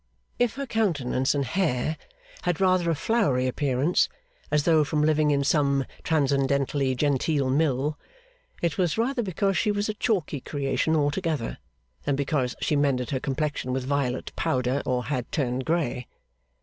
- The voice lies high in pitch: No, medium, 145 Hz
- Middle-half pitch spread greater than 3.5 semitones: Yes, average, 4.0 semitones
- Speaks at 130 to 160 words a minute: Yes, average, 150 wpm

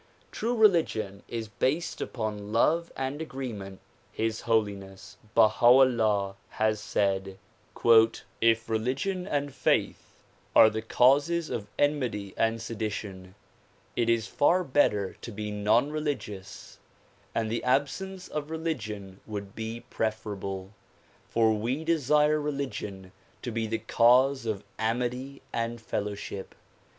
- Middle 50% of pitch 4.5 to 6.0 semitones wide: Yes, average, 4.9 semitones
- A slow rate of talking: Yes, slow, 120 wpm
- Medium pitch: No, low, 115 Hz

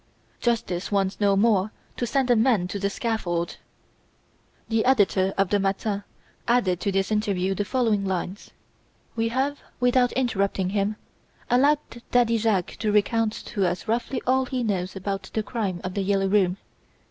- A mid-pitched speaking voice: No, high, 205 Hz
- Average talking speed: Yes, average, 160 wpm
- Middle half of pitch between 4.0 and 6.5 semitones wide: No, average, 3.3 semitones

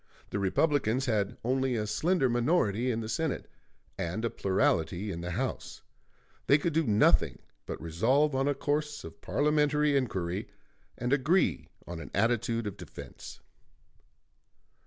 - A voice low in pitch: Yes, low, 120 Hz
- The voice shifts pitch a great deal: Yes, wide, 6.0 semitones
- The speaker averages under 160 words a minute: Yes, average, 140 wpm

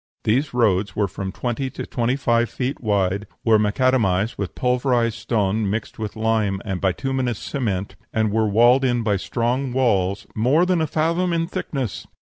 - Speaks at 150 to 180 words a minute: Yes, average, 165 wpm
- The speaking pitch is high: No, low, 115 Hz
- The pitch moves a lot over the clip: No, average, 4.1 semitones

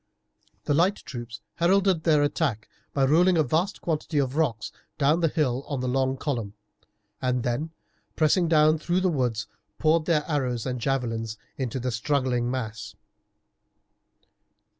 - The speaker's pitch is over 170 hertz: No, medium, 140 Hz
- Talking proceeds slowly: No, average, 145 wpm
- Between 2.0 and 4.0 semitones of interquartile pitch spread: No, average, 4.5 semitones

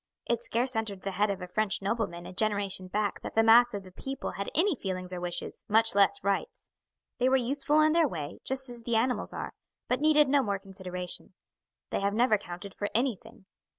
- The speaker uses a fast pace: Yes, fast, 210 wpm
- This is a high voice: Yes, high, 215 Hz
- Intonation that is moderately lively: Yes, average, 4.4 semitones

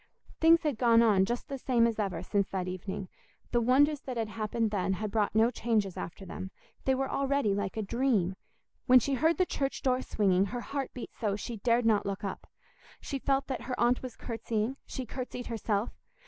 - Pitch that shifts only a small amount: No, average, 4.2 semitones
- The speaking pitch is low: No, high, 230 Hz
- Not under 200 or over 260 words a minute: Yes, fast, 205 wpm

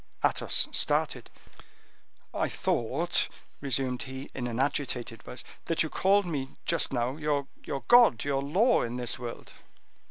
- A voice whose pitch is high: No, low, 135 Hz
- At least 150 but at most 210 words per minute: No, slow, 135 wpm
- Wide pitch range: No, average, 4.1 semitones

